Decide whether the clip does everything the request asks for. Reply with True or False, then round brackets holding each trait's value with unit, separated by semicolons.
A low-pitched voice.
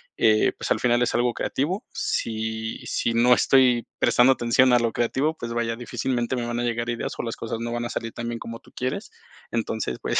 True (120 Hz)